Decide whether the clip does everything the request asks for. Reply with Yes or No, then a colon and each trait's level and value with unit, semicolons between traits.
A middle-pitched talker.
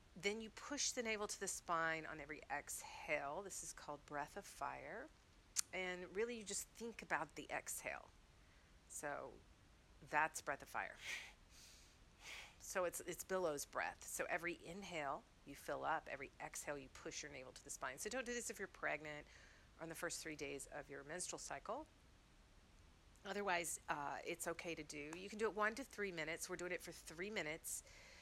Yes: medium, 175 Hz